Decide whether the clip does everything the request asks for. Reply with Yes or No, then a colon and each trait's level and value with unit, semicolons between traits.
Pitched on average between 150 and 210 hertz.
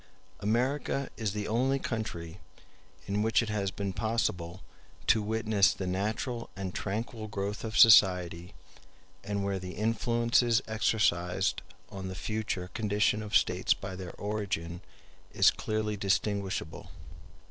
No: low, 105 Hz